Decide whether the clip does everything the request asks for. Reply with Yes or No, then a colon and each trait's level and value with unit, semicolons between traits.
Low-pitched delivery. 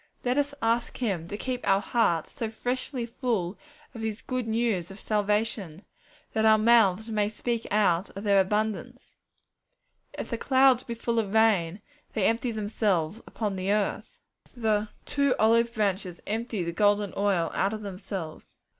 No: high, 215 Hz